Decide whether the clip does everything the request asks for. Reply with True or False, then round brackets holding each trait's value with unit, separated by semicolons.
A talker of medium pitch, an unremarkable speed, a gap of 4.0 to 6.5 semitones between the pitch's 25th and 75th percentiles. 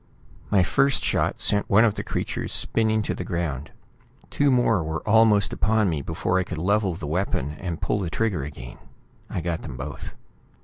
False (95 Hz; 185 wpm; 5.1 semitones)